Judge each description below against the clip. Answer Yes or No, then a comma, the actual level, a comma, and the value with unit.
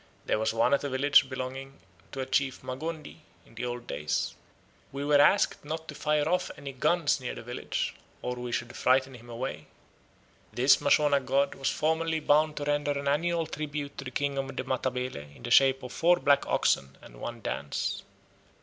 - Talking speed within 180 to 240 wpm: Yes, average, 195 wpm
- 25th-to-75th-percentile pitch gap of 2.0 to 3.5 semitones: Yes, average, 2.9 semitones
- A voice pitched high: No, low, 135 Hz